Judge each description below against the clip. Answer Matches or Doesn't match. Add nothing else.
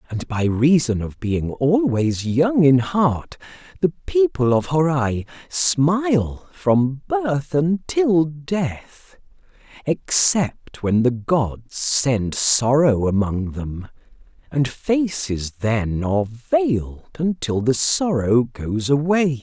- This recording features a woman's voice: Doesn't match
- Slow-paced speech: Matches